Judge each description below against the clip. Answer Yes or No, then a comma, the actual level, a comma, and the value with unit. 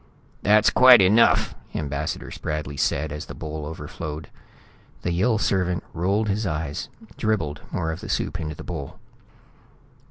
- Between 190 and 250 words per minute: No, average, 145 wpm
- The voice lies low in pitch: Yes, very low, 80 Hz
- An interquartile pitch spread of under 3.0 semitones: No, average, 4.9 semitones